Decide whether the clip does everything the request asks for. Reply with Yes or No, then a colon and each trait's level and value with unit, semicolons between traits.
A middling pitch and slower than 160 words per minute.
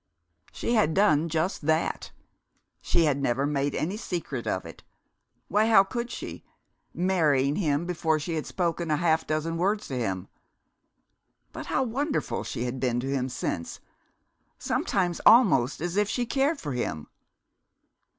Yes: medium, 160 Hz; average, 150 wpm